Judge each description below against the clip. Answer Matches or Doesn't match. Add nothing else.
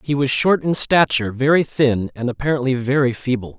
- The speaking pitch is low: Matches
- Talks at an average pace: Matches